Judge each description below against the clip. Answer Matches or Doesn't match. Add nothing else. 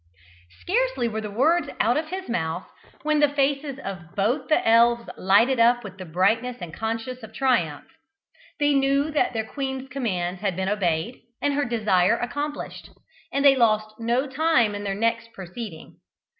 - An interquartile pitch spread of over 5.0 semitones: Matches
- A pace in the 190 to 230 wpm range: Doesn't match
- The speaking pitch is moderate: Doesn't match